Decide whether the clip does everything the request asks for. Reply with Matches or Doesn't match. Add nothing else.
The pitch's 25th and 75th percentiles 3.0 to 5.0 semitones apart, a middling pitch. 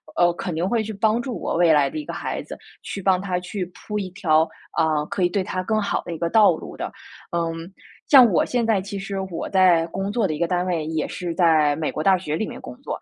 Matches